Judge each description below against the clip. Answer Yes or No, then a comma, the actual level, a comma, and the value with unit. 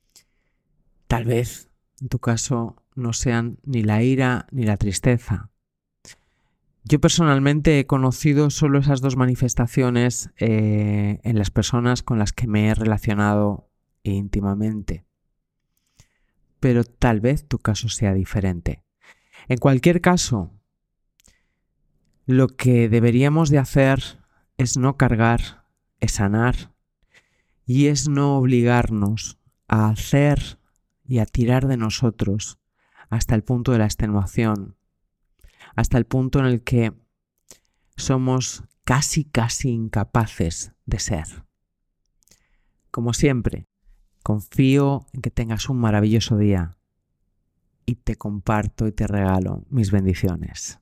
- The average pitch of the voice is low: Yes, low, 115 Hz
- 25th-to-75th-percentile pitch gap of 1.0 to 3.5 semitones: No, average, 4.2 semitones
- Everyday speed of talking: No, slow, 115 wpm